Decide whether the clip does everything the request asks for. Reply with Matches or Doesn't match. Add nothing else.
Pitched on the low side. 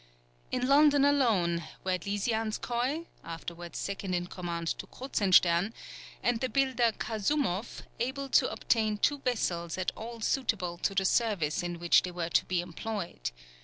Doesn't match